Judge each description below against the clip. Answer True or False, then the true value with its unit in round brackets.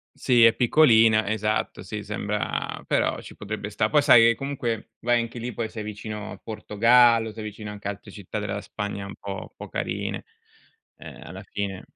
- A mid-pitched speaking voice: False (110 Hz)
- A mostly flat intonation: True (1.9 semitones)